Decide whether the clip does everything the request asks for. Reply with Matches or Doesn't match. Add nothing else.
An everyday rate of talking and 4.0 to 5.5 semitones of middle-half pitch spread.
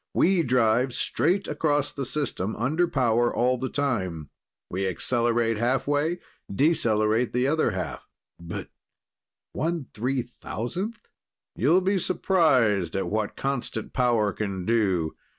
Doesn't match